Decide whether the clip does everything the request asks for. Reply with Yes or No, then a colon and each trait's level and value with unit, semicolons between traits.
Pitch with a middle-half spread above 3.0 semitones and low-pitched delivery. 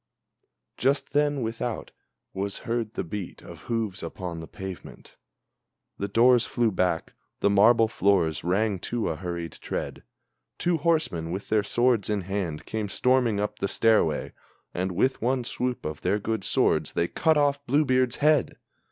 Yes: average, 5.1 semitones; low, 110 Hz